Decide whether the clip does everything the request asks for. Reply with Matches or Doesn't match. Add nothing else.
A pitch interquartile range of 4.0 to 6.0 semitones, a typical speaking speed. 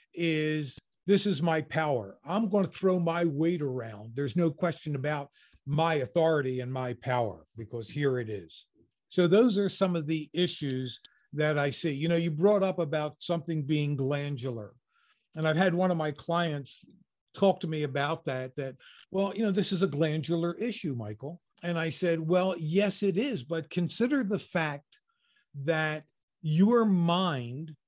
Matches